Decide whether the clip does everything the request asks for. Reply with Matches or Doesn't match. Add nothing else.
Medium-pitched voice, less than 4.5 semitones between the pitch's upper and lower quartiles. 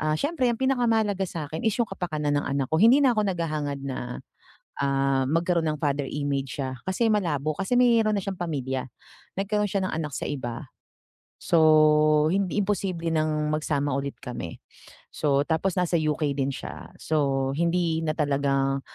Doesn't match